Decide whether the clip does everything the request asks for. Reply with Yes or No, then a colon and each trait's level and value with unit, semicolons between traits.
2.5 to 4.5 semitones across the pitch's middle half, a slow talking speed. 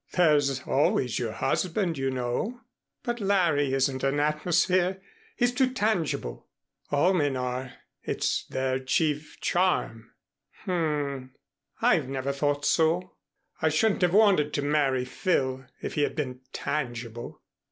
No: average, 5.2 semitones; slow, 130 wpm